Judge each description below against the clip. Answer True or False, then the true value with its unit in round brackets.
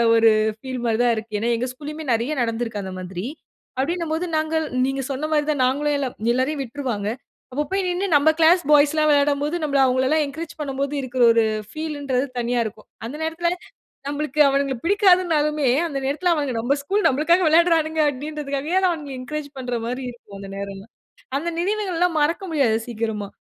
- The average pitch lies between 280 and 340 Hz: True (285 Hz)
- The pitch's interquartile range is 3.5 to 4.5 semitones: True (4.1 semitones)